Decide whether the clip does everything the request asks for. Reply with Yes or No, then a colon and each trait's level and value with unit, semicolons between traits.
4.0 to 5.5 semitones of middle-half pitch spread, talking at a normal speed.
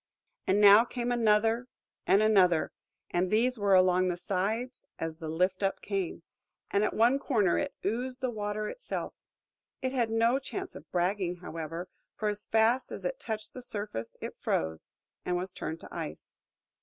Yes: average, 4.5 semitones; average, 170 wpm